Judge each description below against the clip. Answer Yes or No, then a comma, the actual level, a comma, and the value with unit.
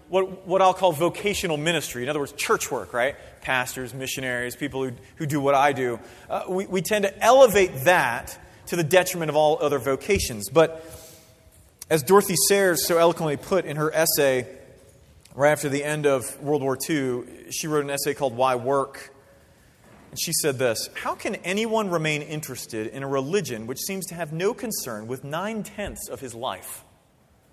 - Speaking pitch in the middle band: Yes, medium, 150 Hz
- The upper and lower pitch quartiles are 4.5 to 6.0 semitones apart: Yes, average, 5.2 semitones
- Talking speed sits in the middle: Yes, average, 185 wpm